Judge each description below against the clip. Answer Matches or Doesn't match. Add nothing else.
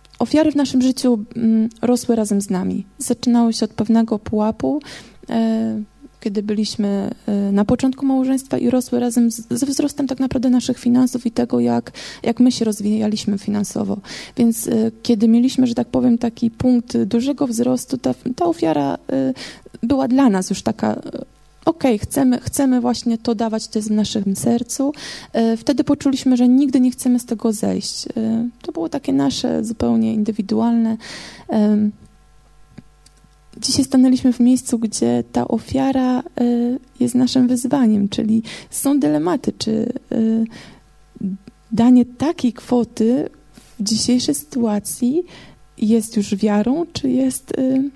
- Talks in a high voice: Matches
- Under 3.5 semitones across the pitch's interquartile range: Matches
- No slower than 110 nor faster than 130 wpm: Doesn't match